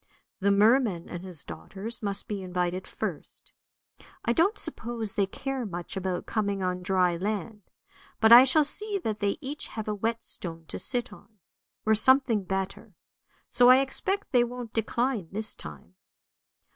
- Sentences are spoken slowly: No, average, 160 wpm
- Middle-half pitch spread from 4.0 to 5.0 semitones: Yes, average, 4.5 semitones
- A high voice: Yes, high, 215 Hz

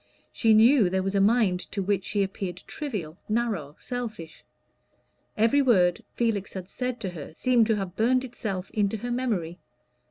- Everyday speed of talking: Yes, average, 165 wpm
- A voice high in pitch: Yes, high, 205 Hz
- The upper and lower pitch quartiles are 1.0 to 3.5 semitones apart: No, average, 4.4 semitones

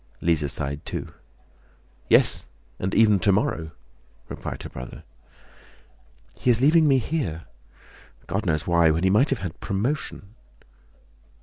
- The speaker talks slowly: Yes, slow, 125 wpm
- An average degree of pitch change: No, wide, 7.0 semitones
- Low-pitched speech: Yes, very low, 95 Hz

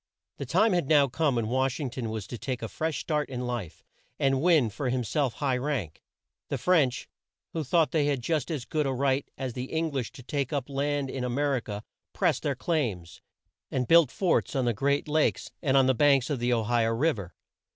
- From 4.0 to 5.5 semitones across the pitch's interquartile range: No, average, 3.4 semitones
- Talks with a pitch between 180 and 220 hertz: No, low, 135 Hz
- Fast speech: Yes, fast, 235 wpm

